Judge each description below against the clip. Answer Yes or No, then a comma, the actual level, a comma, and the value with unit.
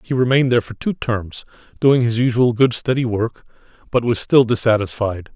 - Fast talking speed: No, average, 180 wpm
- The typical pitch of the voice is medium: No, low, 120 Hz